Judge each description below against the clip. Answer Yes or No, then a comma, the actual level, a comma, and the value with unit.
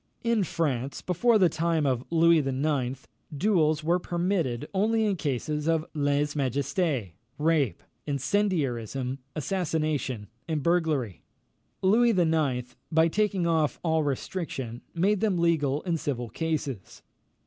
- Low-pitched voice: No, medium, 155 Hz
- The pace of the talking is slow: Yes, slow, 120 wpm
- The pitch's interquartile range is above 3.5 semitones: Yes, average, 4.2 semitones